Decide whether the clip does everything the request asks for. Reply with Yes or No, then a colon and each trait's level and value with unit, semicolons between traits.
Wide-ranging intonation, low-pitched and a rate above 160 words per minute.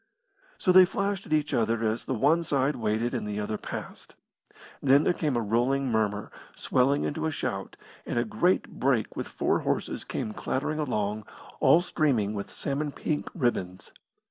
Yes: wide, 5.7 semitones; low, 130 Hz; average, 170 wpm